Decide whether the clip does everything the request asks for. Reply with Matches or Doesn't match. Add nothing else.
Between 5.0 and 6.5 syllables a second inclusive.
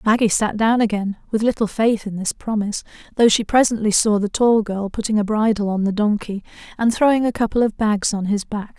Matches